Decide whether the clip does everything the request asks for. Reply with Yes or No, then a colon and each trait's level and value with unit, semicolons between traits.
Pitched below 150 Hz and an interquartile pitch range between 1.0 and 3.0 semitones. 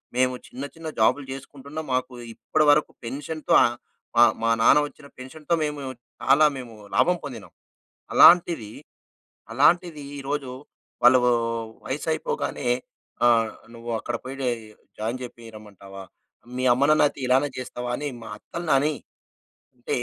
No: low, 135 Hz; average, 3.7 semitones